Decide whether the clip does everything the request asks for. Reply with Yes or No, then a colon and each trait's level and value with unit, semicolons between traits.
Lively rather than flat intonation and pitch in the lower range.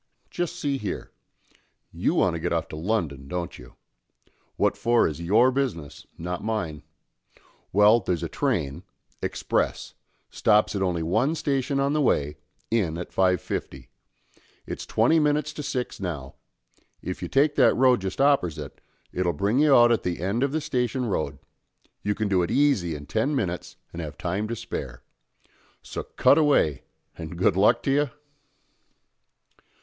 Yes: wide, 7.9 semitones; low, 105 Hz